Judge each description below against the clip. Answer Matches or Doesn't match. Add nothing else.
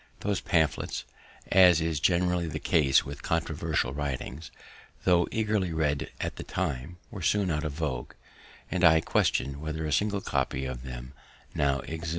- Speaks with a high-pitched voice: Doesn't match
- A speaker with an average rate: Matches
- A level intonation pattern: Doesn't match